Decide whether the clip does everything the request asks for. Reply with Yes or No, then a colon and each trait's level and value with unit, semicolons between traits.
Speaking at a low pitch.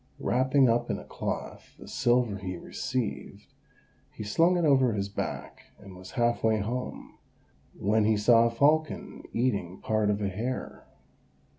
Yes: low, 115 Hz